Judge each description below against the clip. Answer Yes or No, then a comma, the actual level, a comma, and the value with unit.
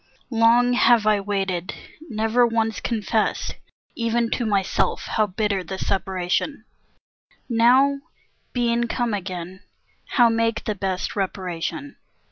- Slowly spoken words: Yes, slow, 110 wpm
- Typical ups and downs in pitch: Yes, average, 3.5 semitones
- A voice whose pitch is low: No, high, 220 Hz